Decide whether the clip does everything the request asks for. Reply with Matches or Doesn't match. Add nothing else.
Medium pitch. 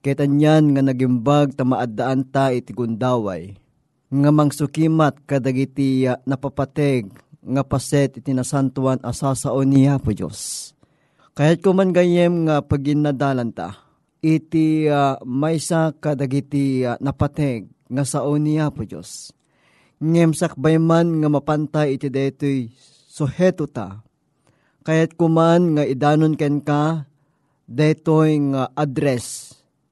Matches